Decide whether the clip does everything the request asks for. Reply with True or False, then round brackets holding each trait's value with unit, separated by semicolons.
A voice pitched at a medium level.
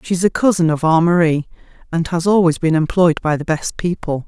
True (165 Hz)